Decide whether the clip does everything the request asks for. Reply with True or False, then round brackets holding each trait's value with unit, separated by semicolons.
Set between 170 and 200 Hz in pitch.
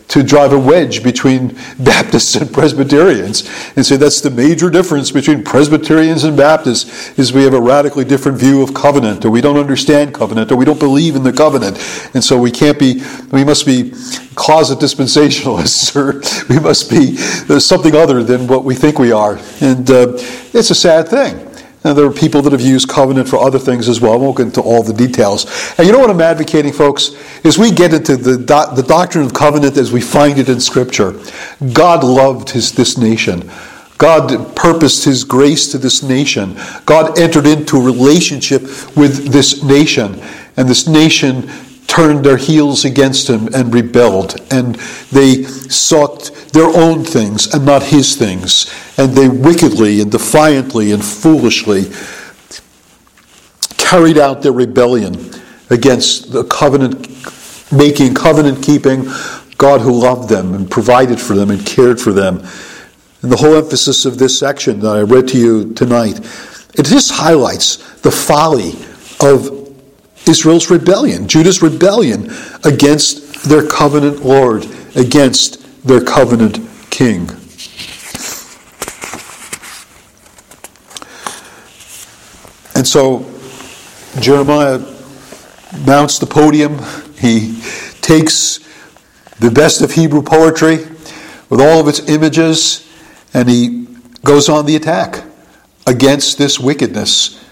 False (140 Hz)